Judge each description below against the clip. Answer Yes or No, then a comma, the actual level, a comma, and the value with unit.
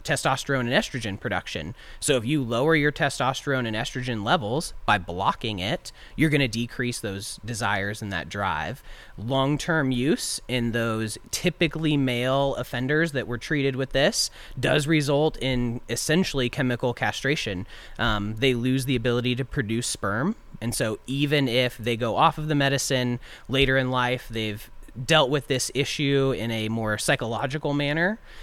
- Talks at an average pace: Yes, average, 160 wpm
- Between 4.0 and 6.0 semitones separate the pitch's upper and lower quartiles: No, average, 3.5 semitones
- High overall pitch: No, low, 130 Hz